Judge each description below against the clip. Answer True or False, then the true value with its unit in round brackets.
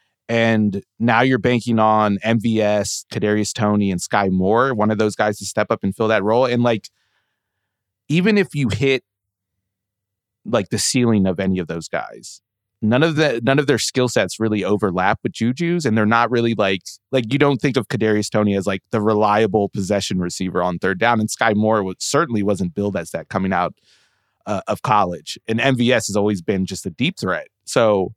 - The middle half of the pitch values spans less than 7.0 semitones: True (2.8 semitones)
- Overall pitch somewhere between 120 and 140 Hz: False (105 Hz)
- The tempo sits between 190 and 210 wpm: True (195 wpm)